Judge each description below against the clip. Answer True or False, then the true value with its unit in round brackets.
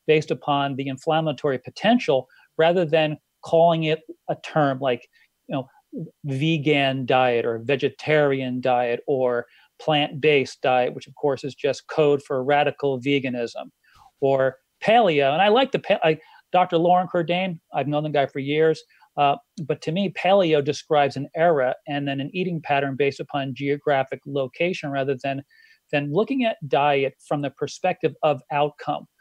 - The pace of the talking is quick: False (155 wpm)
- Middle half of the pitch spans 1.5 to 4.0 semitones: True (3.0 semitones)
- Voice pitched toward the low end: False (145 Hz)